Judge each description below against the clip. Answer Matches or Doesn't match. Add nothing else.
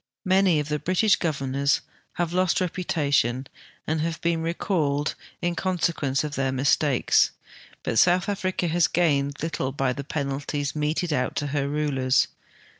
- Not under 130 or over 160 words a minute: Matches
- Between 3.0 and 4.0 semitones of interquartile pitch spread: Matches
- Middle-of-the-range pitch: Matches